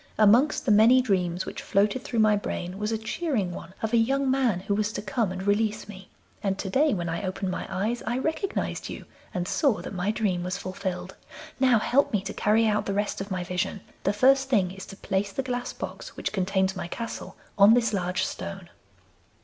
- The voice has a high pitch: Yes, high, 205 Hz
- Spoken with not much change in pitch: No, average, 3.8 semitones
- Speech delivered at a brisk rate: Yes, fast, 215 wpm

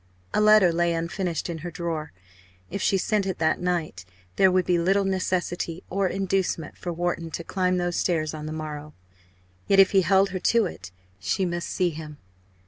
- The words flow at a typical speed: Yes, average, 190 wpm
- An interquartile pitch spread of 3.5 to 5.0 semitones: No, average, 2.7 semitones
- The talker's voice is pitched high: No, medium, 175 Hz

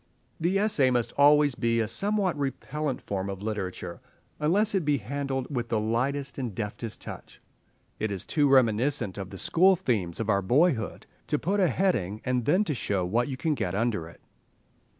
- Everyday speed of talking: Yes, average, 180 wpm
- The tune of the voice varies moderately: No, wide, 5.8 semitones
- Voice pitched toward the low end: Yes, low, 125 Hz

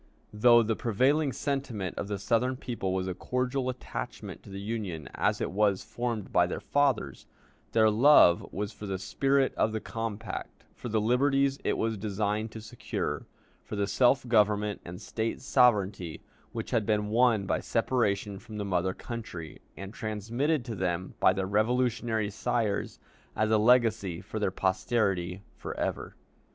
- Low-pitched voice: Yes, low, 110 Hz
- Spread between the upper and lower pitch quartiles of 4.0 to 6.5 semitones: No, average, 3.6 semitones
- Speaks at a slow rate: No, average, 165 wpm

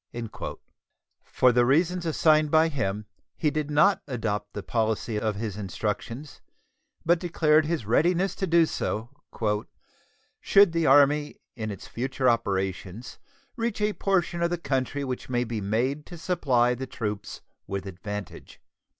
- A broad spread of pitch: Yes, wide, 6.9 semitones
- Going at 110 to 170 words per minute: Yes, average, 140 wpm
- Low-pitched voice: Yes, low, 130 Hz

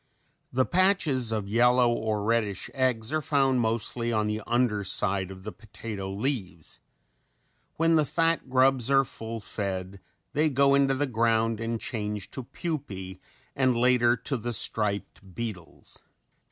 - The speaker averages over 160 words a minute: No, average, 145 wpm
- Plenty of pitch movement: No, average, 4.1 semitones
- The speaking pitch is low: Yes, low, 115 Hz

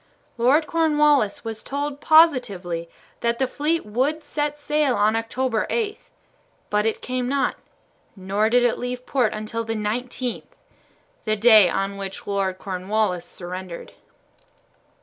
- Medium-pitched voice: No, high, 230 Hz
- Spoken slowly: Yes, slow, 130 wpm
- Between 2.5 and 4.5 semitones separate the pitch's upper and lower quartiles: No, wide, 5.4 semitones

